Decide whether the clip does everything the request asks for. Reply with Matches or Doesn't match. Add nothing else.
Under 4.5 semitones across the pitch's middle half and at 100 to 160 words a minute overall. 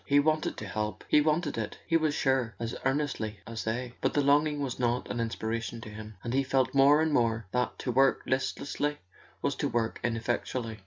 Doesn't match